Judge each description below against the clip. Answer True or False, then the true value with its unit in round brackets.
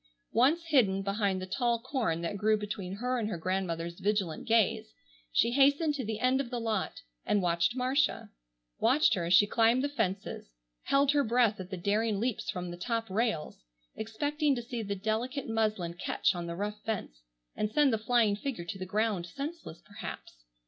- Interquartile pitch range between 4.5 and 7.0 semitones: True (4.8 semitones)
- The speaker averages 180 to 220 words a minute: True (190 wpm)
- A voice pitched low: False (220 Hz)